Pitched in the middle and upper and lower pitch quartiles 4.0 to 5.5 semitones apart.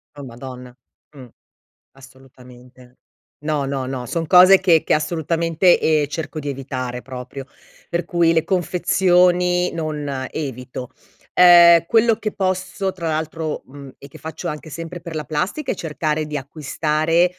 Yes: medium, 155 Hz; average, 4.4 semitones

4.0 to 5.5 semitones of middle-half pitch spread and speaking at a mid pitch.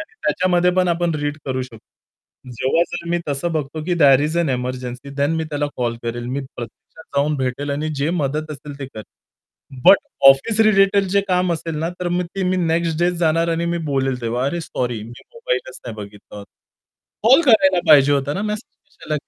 Yes: average, 4.8 semitones; medium, 155 Hz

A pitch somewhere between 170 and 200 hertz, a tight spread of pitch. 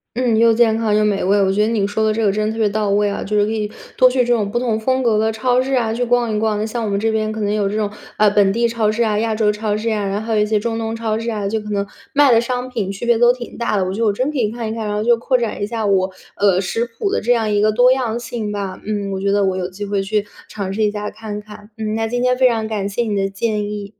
No: high, 215 Hz; narrow, 2.1 semitones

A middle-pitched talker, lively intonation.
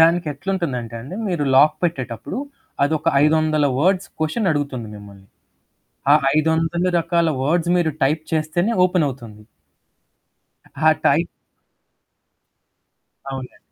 No: medium, 155 Hz; average, 4.1 semitones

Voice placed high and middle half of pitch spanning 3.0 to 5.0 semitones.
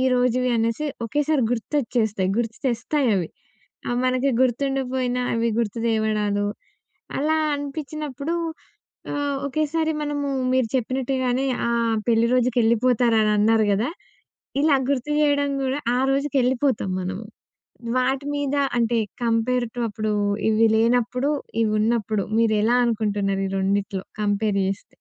Yes: high, 245 Hz; average, 3.7 semitones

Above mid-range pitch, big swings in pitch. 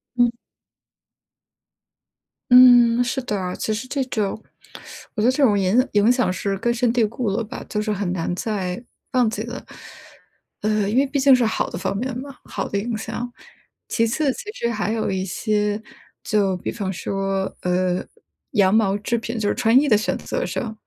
No: high, 220 Hz; average, 3.6 semitones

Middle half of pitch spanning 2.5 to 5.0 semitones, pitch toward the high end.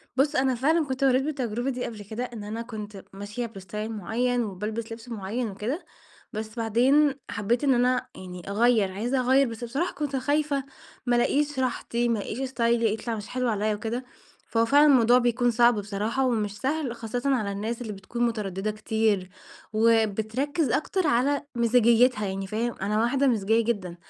Yes: average, 3.2 semitones; high, 235 Hz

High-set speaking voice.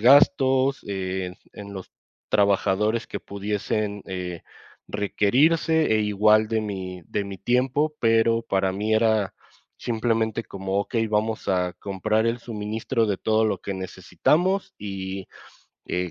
No: low, 105 Hz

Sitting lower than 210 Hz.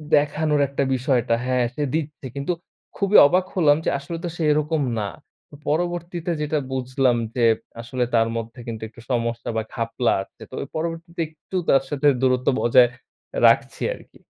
Yes: medium, 140 Hz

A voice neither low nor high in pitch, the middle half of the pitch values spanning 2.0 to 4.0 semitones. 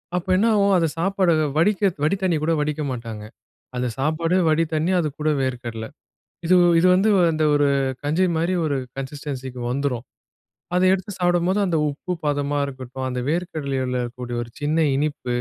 No: medium, 150 Hz; average, 5.0 semitones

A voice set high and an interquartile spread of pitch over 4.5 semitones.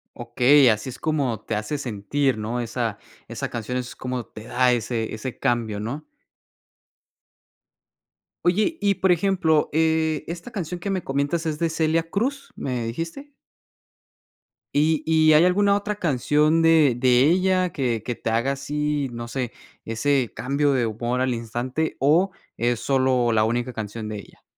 No: low, 135 Hz; average, 5.2 semitones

